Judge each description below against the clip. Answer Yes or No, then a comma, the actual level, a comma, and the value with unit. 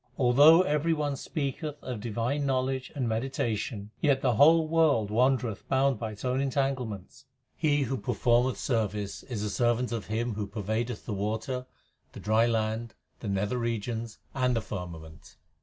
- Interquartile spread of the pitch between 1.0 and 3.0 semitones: No, average, 3.7 semitones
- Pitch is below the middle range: Yes, low, 120 Hz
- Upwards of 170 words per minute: No, average, 160 wpm